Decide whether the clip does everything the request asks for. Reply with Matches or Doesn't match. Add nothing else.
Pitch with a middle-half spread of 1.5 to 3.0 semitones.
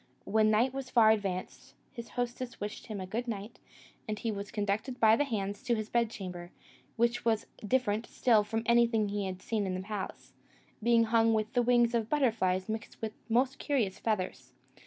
Matches